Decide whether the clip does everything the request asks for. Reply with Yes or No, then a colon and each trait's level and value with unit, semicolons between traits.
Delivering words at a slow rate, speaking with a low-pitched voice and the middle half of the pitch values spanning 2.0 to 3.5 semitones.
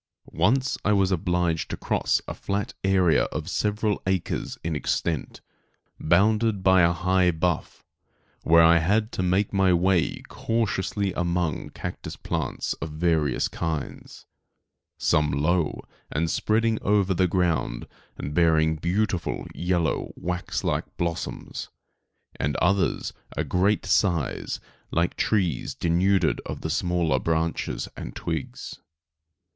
Yes: slow, 125 wpm; very low, 90 Hz; average, 2.9 semitones